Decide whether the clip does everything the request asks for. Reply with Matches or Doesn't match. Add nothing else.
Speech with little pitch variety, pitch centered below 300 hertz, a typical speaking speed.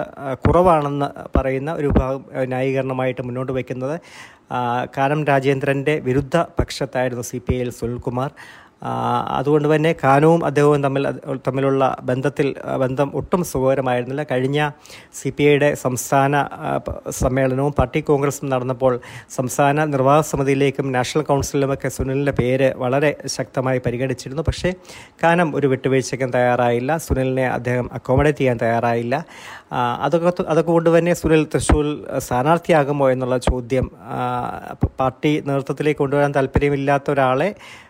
Matches